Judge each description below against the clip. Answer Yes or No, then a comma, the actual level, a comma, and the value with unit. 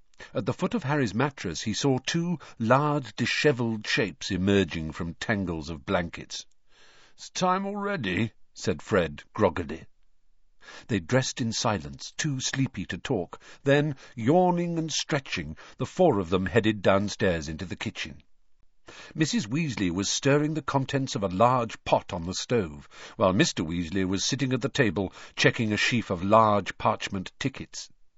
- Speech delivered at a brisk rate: No, average, 155 wpm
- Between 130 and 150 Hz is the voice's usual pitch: No, low, 115 Hz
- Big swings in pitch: Yes, wide, 6.7 semitones